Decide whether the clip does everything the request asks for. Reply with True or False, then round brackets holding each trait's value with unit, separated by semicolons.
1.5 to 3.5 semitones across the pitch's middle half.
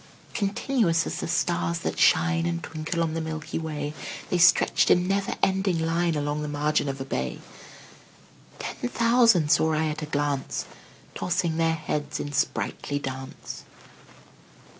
True (3.0 semitones)